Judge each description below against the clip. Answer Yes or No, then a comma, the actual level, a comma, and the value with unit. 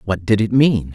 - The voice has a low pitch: Yes, low, 105 Hz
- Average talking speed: No, fast, 255 wpm